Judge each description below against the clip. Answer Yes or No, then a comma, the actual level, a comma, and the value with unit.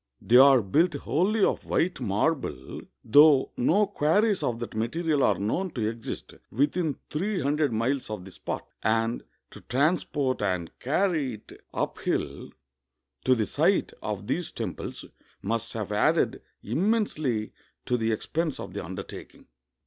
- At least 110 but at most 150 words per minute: Yes, average, 145 wpm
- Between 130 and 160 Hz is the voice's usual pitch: Yes, low, 135 Hz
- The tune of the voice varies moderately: No, wide, 6.3 semitones